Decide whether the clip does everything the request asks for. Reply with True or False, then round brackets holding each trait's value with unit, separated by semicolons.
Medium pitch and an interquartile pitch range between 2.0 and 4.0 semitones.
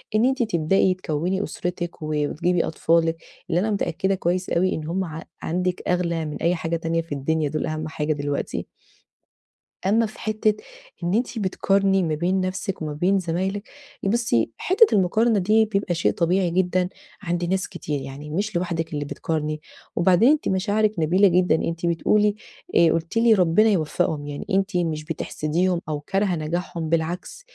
True (175 Hz; 3.3 semitones)